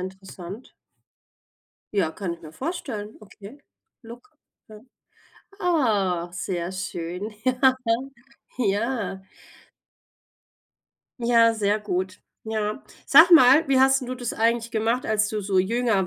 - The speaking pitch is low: No, high, 215 Hz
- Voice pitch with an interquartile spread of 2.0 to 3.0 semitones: No, average, 4.4 semitones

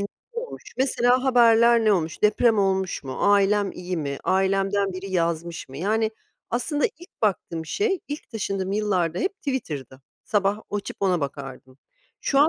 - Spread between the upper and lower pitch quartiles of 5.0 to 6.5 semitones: Yes, average, 5.3 semitones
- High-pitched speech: Yes, high, 200 Hz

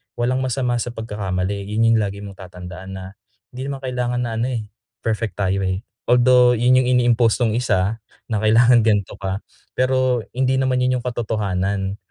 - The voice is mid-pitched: No, low, 115 Hz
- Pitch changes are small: No, average, 3.9 semitones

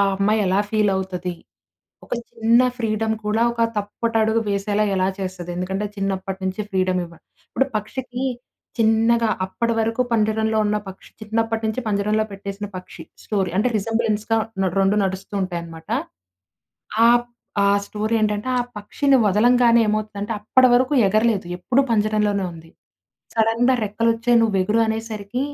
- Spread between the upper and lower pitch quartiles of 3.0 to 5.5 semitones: No, narrow, 2.6 semitones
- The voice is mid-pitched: No, high, 215 Hz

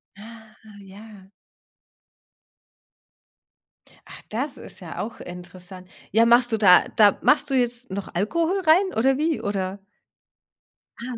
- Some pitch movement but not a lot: Yes, average, 4.8 semitones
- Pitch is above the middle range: Yes, high, 220 Hz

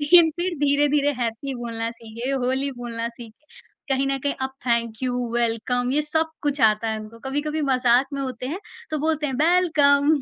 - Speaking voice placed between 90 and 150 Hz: No, very high, 265 Hz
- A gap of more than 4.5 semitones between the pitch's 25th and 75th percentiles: No, average, 3.8 semitones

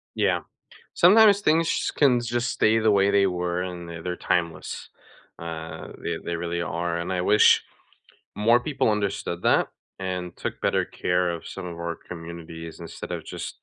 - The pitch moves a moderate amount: Yes, average, 4.1 semitones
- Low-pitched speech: Yes, very low, 90 Hz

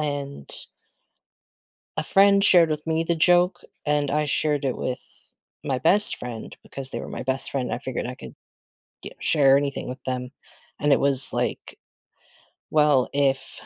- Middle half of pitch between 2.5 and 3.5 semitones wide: Yes, average, 2.8 semitones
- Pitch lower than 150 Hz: Yes, medium, 140 Hz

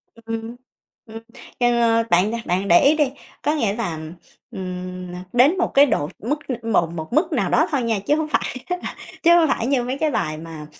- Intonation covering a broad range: Yes, wide, 7.4 semitones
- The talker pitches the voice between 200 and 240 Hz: Yes, high, 230 Hz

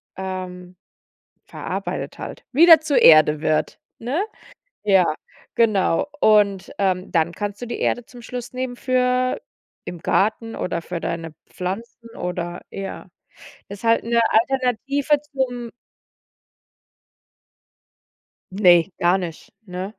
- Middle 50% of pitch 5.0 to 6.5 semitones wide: Yes, wide, 5.4 semitones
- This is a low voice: No, high, 205 Hz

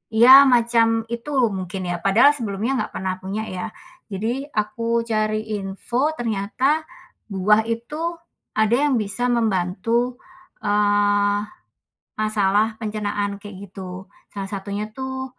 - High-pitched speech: Yes, high, 215 Hz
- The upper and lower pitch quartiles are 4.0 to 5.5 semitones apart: No, average, 2.9 semitones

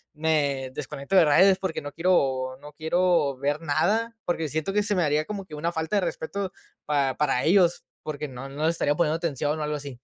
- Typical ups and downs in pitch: Yes, average, 3.5 semitones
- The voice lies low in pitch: No, medium, 155 Hz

